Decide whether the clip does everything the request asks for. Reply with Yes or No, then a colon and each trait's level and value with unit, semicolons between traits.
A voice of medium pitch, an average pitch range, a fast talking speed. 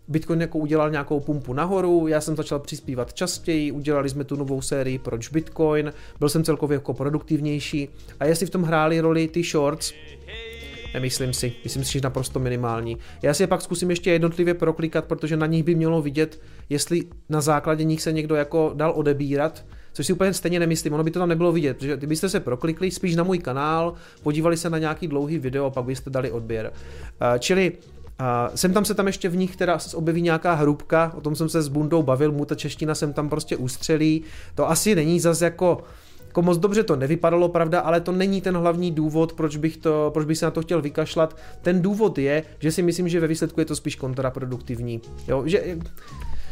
Yes: medium, 155 Hz; average, 3.0 semitones; fast, 205 wpm